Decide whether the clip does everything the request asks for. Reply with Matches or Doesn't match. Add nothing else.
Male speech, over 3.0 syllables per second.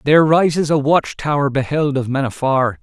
Matches